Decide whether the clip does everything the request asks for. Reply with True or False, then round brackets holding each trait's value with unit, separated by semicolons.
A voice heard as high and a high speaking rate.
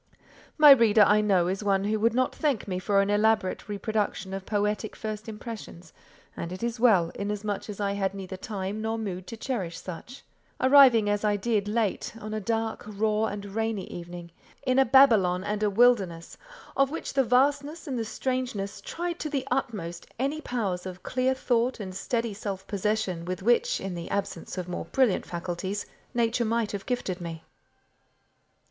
False (210 Hz; 180 wpm)